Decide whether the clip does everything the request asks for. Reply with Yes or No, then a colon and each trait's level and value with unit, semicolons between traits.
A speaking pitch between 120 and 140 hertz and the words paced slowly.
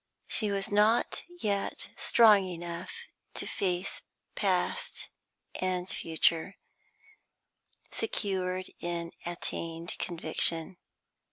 No: medium, 185 Hz; slow, 80 wpm